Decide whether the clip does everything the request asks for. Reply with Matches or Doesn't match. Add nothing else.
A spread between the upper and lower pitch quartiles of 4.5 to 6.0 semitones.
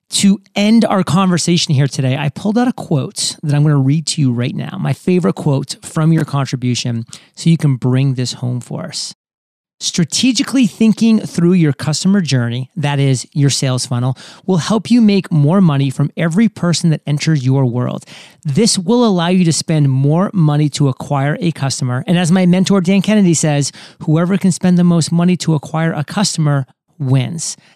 Matches